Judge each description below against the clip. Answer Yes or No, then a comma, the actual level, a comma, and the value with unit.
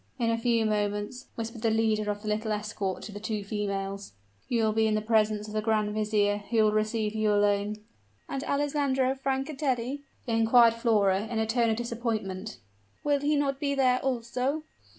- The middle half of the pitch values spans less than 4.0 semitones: Yes, average, 3.0 semitones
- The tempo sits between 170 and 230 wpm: Yes, average, 185 wpm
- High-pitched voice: Yes, high, 220 Hz